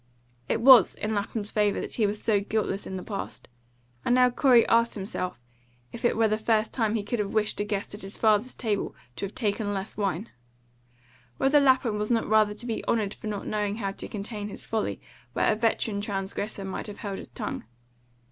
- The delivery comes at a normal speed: No, fast, 210 wpm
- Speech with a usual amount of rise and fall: No, narrow, 2.0 semitones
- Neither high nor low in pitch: No, high, 210 Hz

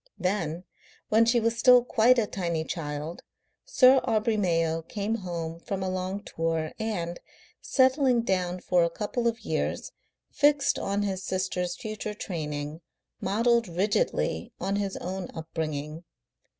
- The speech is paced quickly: No, slow, 135 wpm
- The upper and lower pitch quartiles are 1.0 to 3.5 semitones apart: No, average, 5.3 semitones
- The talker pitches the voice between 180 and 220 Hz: Yes, high, 190 Hz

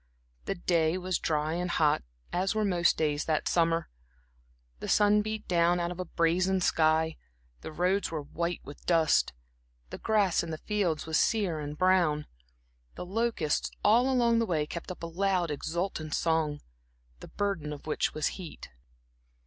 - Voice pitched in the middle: Yes, medium, 170 Hz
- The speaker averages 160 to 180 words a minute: Yes, average, 165 wpm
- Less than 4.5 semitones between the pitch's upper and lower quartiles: Yes, average, 3.4 semitones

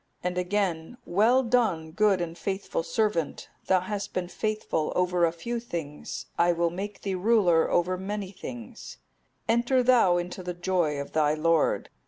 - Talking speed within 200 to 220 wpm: No, average, 165 wpm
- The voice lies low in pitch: No, medium, 185 Hz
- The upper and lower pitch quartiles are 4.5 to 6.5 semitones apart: No, average, 3.8 semitones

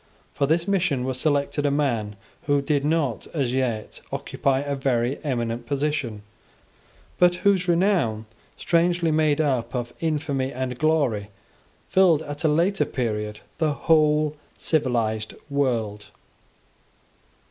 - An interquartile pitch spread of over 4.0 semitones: Yes, average, 4.7 semitones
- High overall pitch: No, medium, 140 Hz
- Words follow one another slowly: Yes, slow, 125 wpm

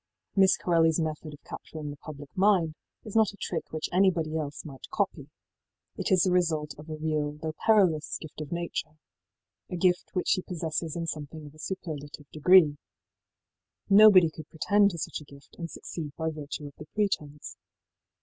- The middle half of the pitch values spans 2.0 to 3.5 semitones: Yes, average, 3.2 semitones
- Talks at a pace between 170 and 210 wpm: Yes, average, 180 wpm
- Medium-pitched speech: Yes, medium, 160 Hz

